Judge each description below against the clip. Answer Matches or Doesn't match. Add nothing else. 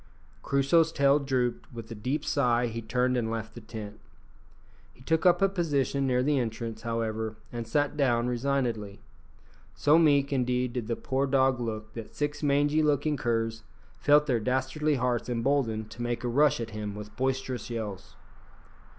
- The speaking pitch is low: Matches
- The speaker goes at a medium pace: Matches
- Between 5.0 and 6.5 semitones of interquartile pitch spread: Doesn't match